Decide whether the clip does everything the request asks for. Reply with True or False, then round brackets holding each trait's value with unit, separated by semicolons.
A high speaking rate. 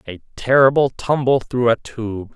False (155 wpm)